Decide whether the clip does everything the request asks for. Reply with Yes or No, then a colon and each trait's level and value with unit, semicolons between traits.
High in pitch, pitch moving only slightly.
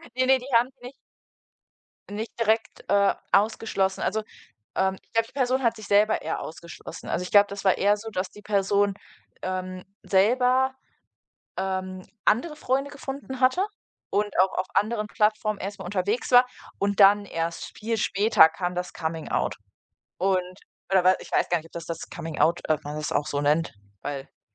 No: high, 200 Hz; average, 3.6 semitones